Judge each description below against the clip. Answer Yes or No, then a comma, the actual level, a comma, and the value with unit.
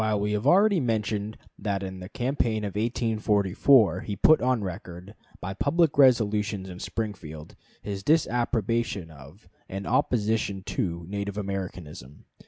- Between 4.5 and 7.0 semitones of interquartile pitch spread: No, average, 3.5 semitones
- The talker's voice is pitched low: Yes, low, 105 Hz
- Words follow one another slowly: Yes, slow, 130 wpm